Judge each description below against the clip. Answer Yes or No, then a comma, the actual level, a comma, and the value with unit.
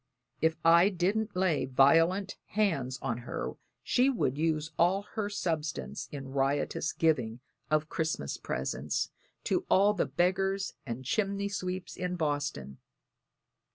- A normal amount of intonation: No, wide, 5.8 semitones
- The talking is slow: Yes, slow, 125 wpm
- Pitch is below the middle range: No, medium, 165 Hz